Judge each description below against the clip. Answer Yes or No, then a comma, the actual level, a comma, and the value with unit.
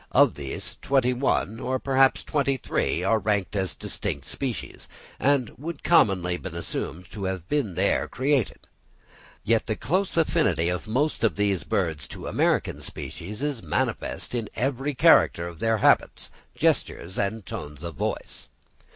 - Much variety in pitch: Yes, wide, 6.9 semitones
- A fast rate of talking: No, average, 150 wpm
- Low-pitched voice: Yes, low, 110 Hz